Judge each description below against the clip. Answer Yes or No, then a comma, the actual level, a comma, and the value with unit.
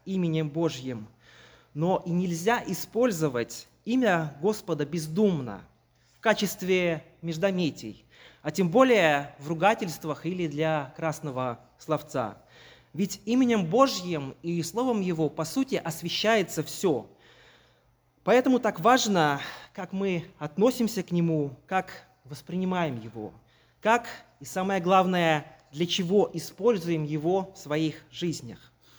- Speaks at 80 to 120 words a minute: Yes, slow, 110 wpm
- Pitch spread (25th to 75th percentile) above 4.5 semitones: No, average, 4.2 semitones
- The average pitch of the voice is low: No, medium, 170 Hz